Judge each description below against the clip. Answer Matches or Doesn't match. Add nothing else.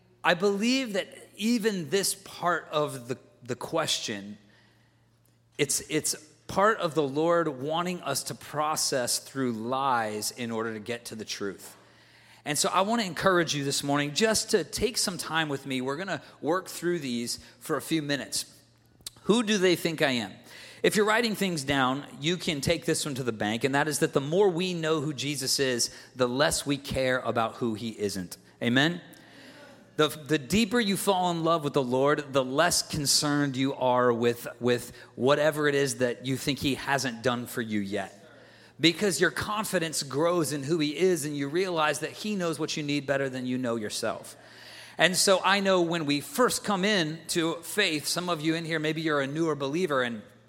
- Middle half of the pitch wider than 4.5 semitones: Matches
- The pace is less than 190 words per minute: Doesn't match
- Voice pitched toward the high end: Doesn't match